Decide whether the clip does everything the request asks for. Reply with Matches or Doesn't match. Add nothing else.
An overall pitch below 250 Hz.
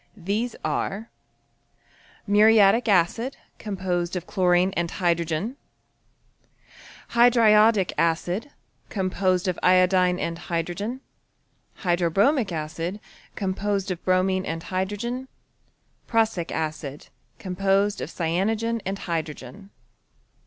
Matches